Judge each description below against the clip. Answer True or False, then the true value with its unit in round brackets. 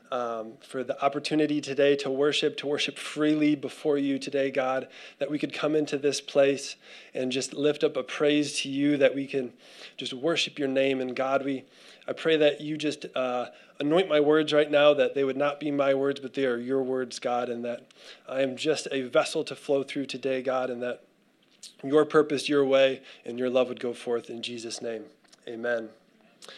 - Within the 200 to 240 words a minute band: True (205 wpm)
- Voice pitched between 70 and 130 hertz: False (140 Hz)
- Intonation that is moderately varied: False (2.2 semitones)